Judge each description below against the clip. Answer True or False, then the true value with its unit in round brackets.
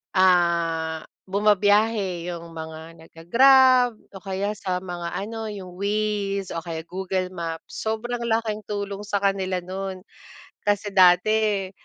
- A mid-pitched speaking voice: False (195 Hz)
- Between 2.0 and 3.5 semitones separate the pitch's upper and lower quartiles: True (3.0 semitones)